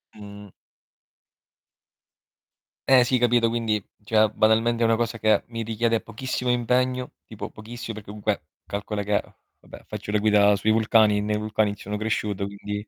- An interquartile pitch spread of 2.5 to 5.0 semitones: No, narrow, 1.9 semitones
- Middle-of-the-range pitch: No, low, 110 Hz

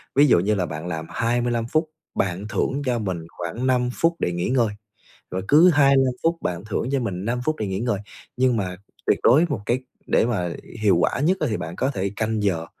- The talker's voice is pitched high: No, low, 115 Hz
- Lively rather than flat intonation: Yes, wide, 5.8 semitones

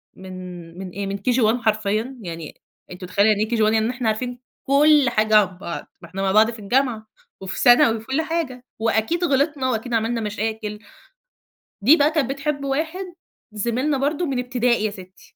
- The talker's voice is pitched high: Yes, high, 225 Hz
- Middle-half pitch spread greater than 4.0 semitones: Yes, average, 4.5 semitones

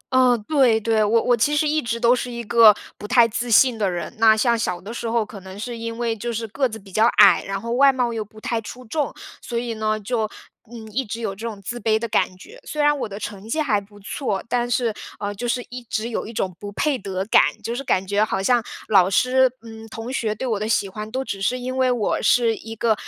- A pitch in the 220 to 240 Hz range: Yes, high, 225 Hz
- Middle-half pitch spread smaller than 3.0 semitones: Yes, narrow, 2.6 semitones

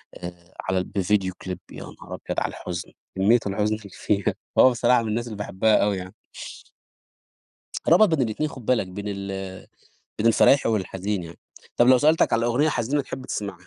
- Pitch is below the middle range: Yes, low, 105 Hz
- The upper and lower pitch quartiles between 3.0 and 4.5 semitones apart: Yes, average, 4.2 semitones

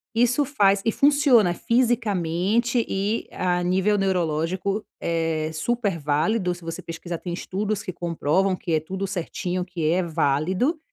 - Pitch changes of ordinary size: Yes, average, 4.1 semitones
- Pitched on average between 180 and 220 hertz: Yes, medium, 185 Hz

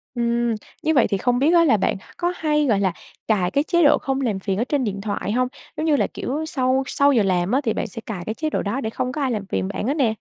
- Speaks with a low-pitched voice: No, high, 245 Hz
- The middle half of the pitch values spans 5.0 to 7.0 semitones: Yes, wide, 5.4 semitones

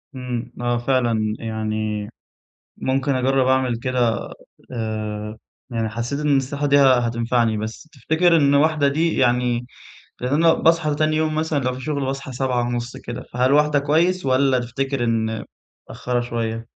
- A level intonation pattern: No, average, 3.3 semitones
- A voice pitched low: Yes, low, 130 Hz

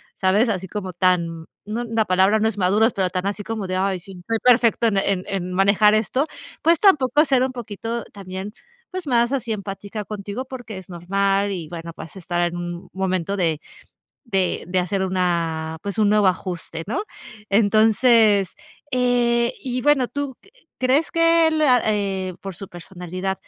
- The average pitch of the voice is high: Yes, high, 200 Hz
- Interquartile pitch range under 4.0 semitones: No, average, 4.3 semitones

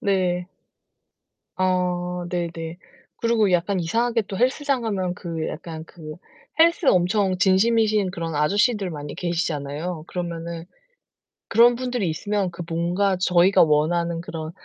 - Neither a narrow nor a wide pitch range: Yes, average, 3.5 semitones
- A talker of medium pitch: Yes, medium, 180 Hz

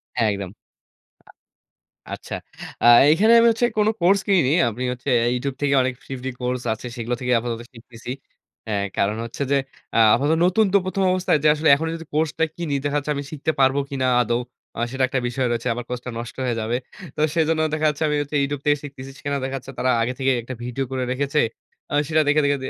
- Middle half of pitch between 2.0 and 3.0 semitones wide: No, average, 3.8 semitones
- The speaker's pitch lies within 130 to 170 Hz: Yes, low, 135 Hz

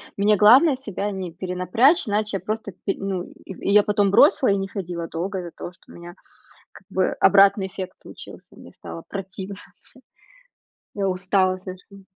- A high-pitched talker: Yes, high, 195 Hz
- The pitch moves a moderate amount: No, narrow, 2.1 semitones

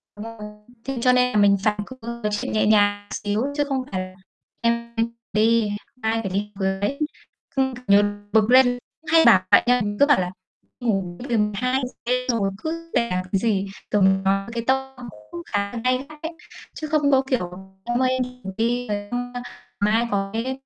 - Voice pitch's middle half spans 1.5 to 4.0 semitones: Yes, average, 3.7 semitones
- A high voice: Yes, high, 230 Hz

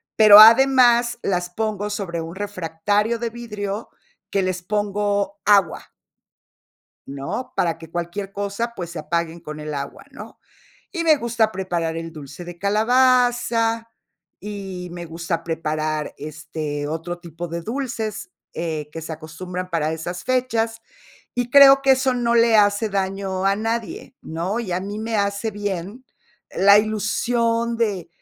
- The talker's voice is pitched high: Yes, high, 200 Hz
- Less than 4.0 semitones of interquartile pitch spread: No, average, 5.1 semitones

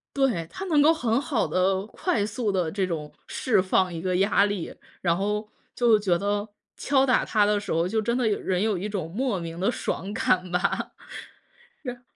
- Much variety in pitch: No, average, 4.3 semitones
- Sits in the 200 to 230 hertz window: Yes, high, 205 Hz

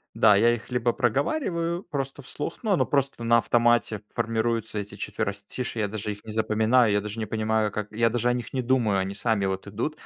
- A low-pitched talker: Yes, low, 115 Hz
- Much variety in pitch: No, average, 2.9 semitones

